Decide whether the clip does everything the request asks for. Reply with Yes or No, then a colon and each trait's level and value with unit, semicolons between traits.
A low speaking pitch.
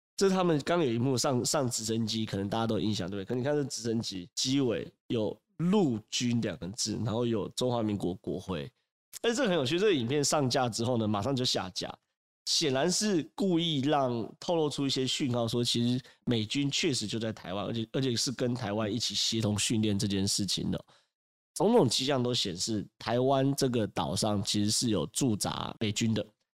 Yes: low, 120 Hz